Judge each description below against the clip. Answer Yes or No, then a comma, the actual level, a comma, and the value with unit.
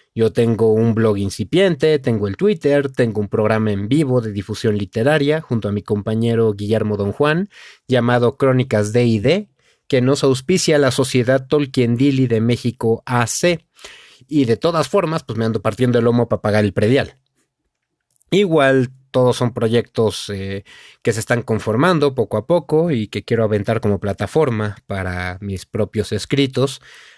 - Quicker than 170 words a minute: No, average, 165 wpm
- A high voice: No, low, 120 Hz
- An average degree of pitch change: Yes, average, 4.5 semitones